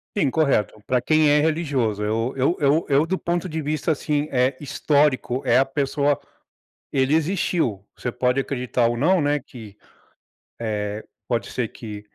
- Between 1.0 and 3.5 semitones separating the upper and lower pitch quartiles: No, average, 4.1 semitones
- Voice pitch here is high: No, low, 135 Hz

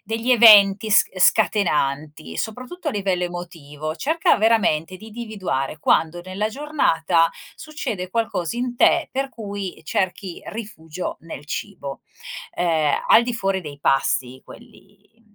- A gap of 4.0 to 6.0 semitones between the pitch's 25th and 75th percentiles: Yes, wide, 5.6 semitones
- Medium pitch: No, high, 195 Hz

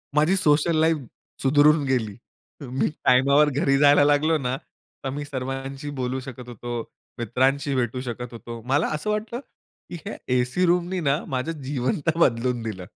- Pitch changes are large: No, average, 3.2 semitones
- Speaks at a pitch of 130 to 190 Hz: Yes, low, 135 Hz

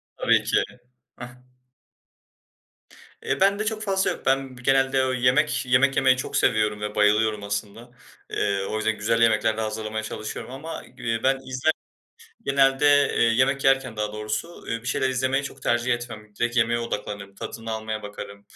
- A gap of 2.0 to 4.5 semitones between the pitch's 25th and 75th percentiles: Yes, average, 3.8 semitones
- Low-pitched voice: Yes, low, 120 Hz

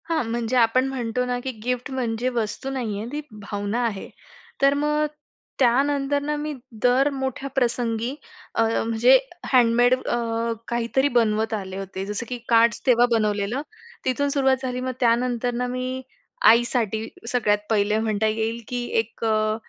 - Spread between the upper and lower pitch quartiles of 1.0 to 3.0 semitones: Yes, narrow, 2.6 semitones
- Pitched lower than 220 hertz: No, high, 240 Hz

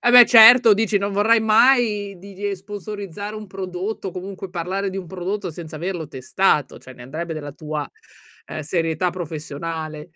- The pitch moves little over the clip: No, average, 4.1 semitones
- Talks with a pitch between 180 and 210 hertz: Yes, high, 190 Hz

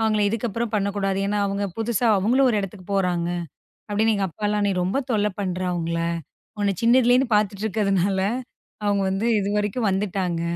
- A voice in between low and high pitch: No, high, 205 Hz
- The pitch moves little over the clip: Yes, narrow, 2.2 semitones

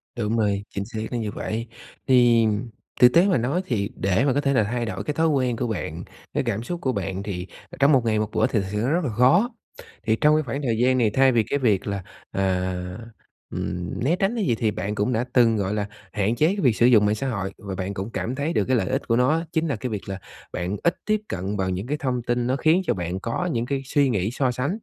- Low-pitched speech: Yes, low, 120 Hz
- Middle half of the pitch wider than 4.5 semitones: Yes, average, 5.0 semitones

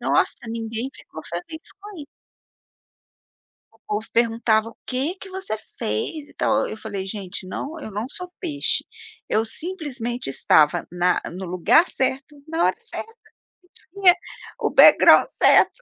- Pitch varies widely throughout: Yes, wide, 7.0 semitones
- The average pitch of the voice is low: No, high, 245 Hz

